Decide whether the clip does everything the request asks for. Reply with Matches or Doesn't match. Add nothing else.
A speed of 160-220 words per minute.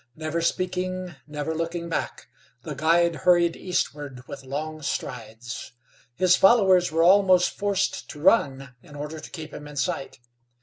Doesn't match